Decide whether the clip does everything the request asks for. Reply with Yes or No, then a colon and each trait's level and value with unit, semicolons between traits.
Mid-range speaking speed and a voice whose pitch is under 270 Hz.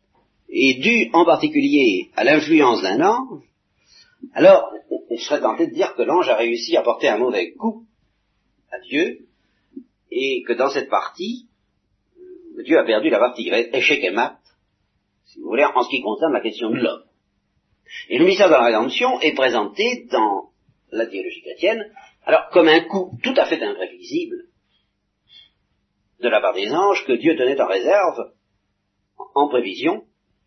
No: average, 160 wpm; very high, 290 Hz